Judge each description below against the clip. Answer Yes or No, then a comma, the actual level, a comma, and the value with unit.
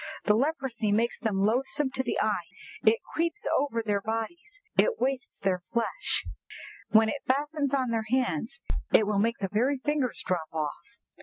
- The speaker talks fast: No, average, 165 wpm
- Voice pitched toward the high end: Yes, high, 235 Hz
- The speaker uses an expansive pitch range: No, average, 4.5 semitones